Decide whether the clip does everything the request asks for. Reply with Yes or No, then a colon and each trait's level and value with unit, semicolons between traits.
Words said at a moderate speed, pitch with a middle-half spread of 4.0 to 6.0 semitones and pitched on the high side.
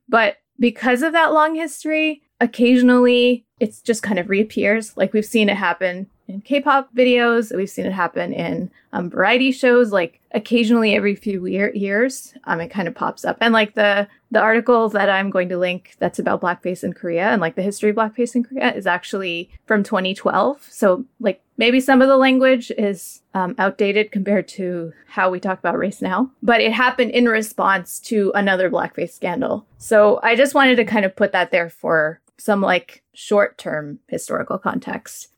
Yes: average, 185 wpm; average, 4.5 semitones; high, 215 Hz